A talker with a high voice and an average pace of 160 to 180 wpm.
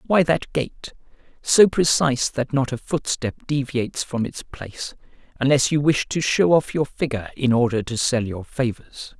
No: low, 135 Hz; average, 175 wpm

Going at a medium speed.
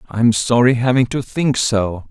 Yes: average, 170 wpm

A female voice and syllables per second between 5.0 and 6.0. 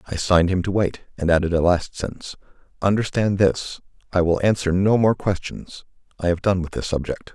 No: male; 5.5 syllables/s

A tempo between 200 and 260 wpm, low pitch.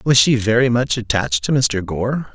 Yes: fast, 205 wpm; low, 115 Hz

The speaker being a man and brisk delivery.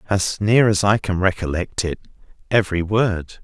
No: male; average, 155 wpm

